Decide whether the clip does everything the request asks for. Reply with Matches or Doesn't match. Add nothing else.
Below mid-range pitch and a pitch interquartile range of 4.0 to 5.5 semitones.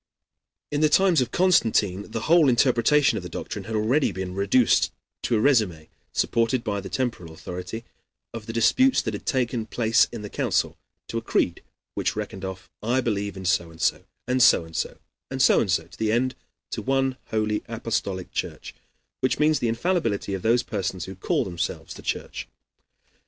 Matches